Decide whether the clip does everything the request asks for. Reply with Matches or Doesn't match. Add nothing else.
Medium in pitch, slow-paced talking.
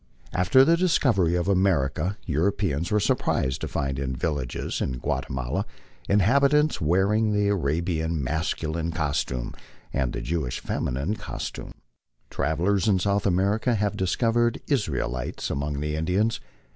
Doesn't match